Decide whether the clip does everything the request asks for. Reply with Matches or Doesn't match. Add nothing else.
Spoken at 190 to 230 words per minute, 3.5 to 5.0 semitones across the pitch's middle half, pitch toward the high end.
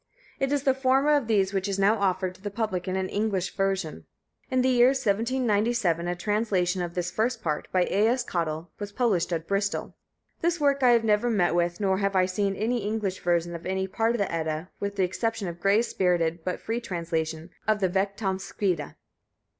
Matches